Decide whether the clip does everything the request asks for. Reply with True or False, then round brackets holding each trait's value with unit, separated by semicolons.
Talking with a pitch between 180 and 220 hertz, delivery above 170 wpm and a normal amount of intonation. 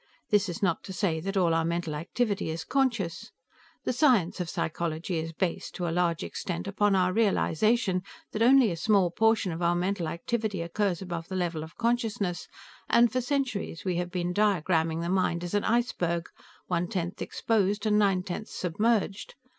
True (185 Hz; 180 wpm; 3.9 semitones)